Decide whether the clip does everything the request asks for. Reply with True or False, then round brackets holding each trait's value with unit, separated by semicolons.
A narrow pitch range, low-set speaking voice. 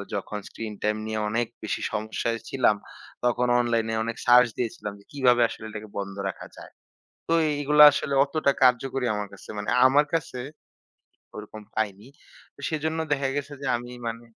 False (3.9 semitones; 120 Hz)